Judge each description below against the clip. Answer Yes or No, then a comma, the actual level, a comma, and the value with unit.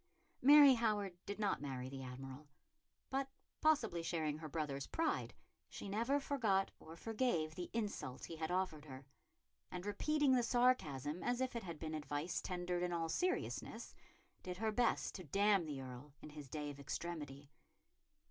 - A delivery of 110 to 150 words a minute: No, average, 165 wpm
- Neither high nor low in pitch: Yes, medium, 175 Hz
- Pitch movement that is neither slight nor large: No, wide, 7.3 semitones